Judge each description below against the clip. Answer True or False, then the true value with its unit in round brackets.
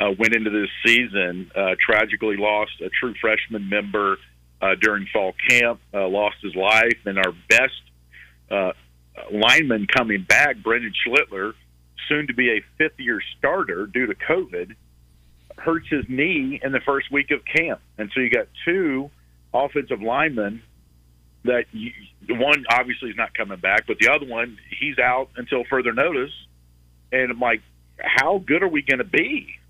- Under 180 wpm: True (165 wpm)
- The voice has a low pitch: True (105 Hz)